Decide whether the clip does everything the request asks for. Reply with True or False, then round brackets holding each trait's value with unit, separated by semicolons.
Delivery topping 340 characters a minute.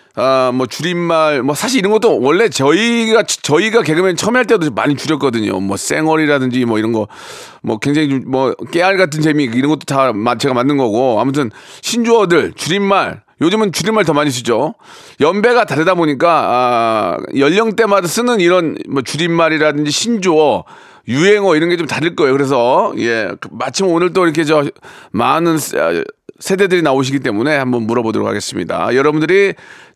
True (355 characters per minute)